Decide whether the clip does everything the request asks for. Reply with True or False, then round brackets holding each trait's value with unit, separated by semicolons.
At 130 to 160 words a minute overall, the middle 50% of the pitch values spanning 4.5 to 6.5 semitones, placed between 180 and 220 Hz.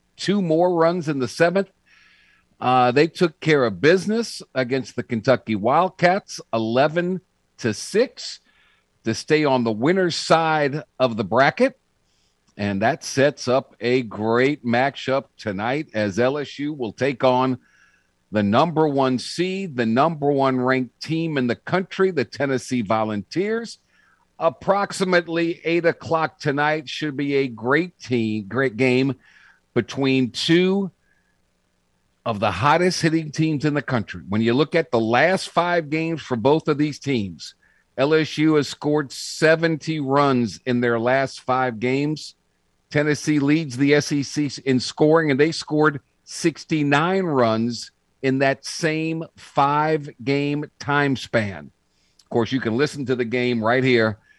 False (140 wpm; 4.8 semitones; 140 Hz)